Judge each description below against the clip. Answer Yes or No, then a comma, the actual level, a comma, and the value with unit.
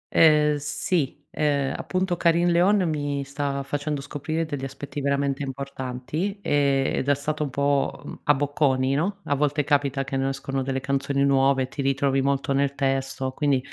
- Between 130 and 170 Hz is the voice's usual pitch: Yes, medium, 140 Hz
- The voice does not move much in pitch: Yes, narrow, 1.6 semitones